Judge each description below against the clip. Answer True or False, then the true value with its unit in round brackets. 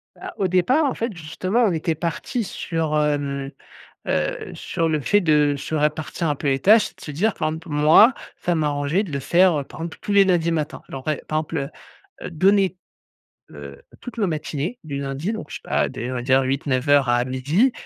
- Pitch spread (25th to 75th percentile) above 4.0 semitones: True (4.7 semitones)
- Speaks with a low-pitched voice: False (155 Hz)